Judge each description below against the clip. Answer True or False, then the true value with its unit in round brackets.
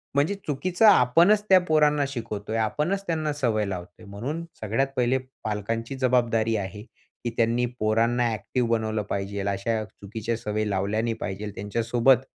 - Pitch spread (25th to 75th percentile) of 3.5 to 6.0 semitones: True (4.2 semitones)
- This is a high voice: False (115 Hz)